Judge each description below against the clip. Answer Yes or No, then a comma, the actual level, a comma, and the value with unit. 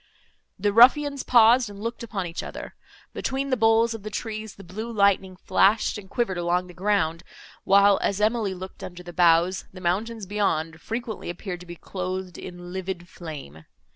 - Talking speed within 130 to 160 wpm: No, average, 175 wpm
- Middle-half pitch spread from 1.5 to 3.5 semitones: No, average, 3.9 semitones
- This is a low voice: No, high, 195 Hz